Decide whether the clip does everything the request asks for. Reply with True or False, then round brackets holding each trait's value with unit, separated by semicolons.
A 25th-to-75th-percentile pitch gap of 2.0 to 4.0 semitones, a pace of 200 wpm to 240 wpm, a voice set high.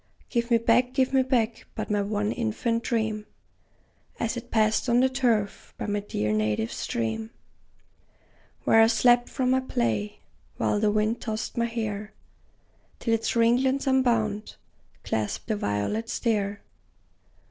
False (2.7 semitones; 145 wpm; 225 Hz)